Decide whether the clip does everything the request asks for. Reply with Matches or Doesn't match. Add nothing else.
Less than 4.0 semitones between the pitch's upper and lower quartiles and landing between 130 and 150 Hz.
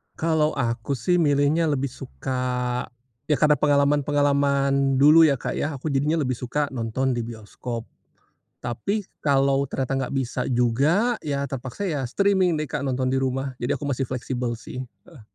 Matches